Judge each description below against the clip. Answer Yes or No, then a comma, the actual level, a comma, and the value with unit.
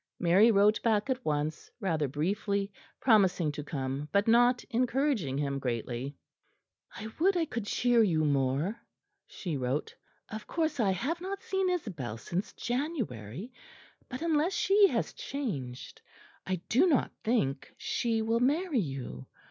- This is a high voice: Yes, high, 205 Hz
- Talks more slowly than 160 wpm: Yes, average, 140 wpm